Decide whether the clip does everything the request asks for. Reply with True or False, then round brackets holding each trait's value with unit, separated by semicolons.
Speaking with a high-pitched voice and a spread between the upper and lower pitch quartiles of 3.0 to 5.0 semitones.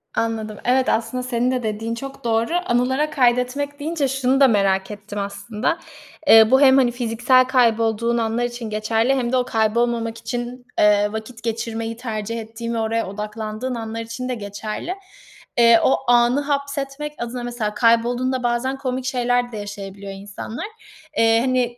False (235 Hz; 2.4 semitones)